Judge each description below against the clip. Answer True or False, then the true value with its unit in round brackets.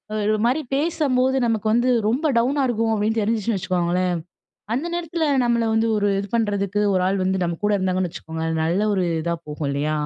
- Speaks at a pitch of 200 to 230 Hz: True (210 Hz)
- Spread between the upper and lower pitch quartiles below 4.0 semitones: False (4.6 semitones)